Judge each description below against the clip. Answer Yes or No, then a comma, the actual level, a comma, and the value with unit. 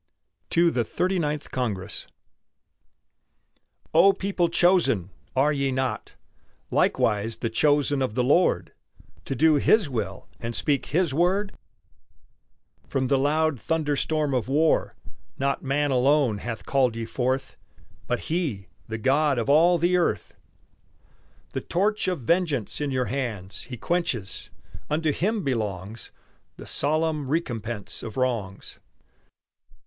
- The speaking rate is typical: No, slow, 130 wpm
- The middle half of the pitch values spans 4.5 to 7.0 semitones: Yes, wide, 5.5 semitones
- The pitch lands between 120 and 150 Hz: Yes, medium, 140 Hz